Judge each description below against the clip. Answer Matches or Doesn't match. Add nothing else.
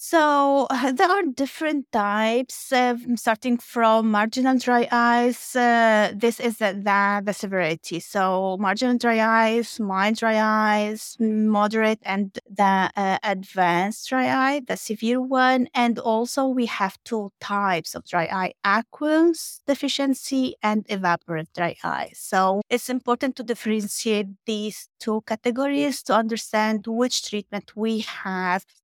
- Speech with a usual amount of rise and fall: Matches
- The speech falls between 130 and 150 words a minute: Matches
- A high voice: Matches